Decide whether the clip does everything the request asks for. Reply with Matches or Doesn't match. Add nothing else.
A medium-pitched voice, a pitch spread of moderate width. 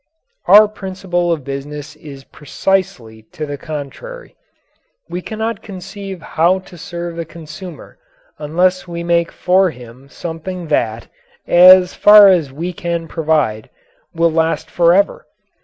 Matches